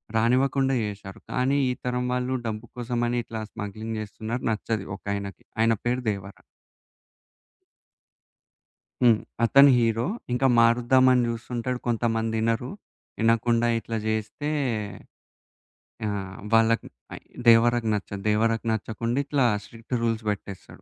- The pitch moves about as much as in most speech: No, narrow, 2.0 semitones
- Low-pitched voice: Yes, low, 115 Hz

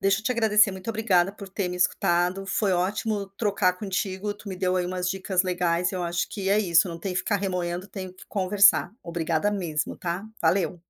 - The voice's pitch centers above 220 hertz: No, medium, 185 Hz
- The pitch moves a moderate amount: No, narrow, 2.1 semitones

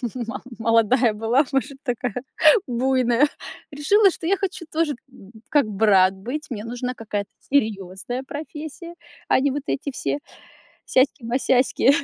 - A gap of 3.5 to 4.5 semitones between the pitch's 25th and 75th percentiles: Yes, average, 4.2 semitones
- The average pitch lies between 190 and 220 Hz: No, very high, 255 Hz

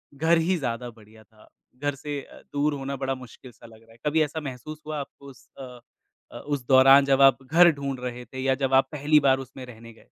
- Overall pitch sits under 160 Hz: Yes, low, 135 Hz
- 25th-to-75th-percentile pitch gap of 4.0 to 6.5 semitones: No, narrow, 2.6 semitones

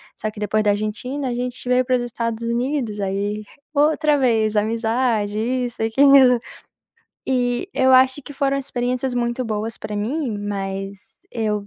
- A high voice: Yes, high, 240 Hz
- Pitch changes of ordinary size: Yes, average, 3.3 semitones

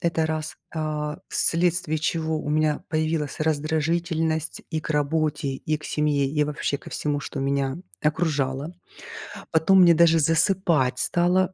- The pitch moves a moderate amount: No, narrow, 1.7 semitones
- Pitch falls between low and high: Yes, medium, 155 Hz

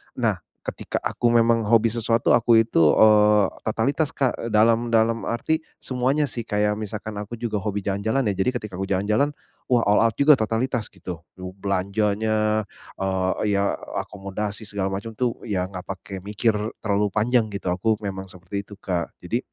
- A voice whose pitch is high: No, low, 105 Hz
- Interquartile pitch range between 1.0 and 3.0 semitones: Yes, narrow, 2.6 semitones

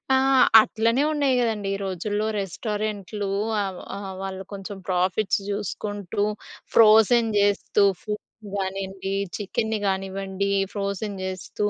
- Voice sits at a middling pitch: No, high, 200 Hz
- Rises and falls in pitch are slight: Yes, narrow, 1.9 semitones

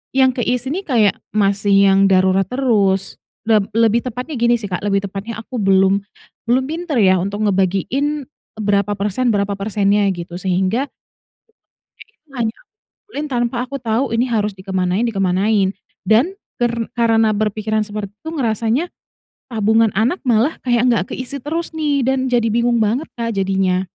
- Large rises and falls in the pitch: No, average, 4.0 semitones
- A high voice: Yes, high, 220 Hz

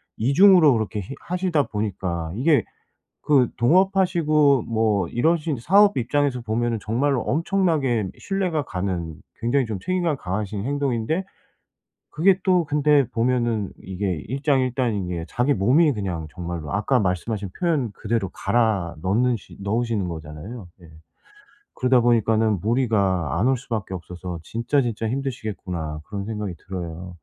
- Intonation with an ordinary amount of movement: No, wide, 6.5 semitones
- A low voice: Yes, low, 115 Hz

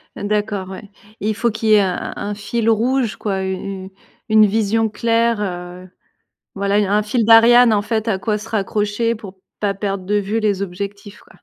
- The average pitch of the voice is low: No, high, 210 Hz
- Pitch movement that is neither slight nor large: No, narrow, 2.2 semitones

